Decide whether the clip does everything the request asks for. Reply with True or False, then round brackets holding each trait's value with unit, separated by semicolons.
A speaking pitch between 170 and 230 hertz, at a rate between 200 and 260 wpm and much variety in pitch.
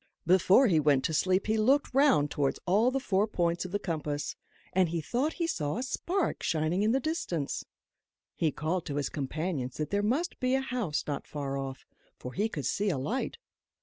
True (185 Hz; 205 wpm; 8.3 semitones)